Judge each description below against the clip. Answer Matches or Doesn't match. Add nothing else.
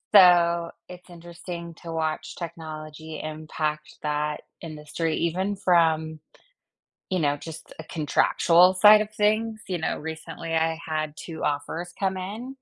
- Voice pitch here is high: Doesn't match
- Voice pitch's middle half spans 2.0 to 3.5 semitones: Matches